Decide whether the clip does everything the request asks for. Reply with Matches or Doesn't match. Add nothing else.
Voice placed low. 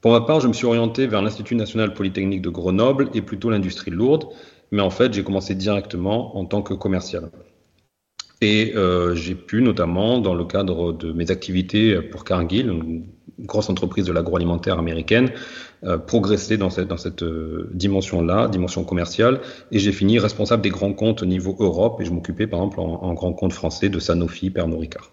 Matches